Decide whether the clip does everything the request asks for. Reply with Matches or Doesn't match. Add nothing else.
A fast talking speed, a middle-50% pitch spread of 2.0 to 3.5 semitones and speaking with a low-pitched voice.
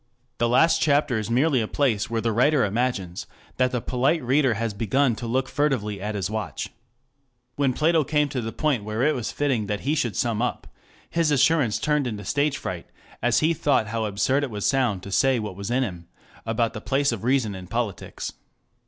Doesn't match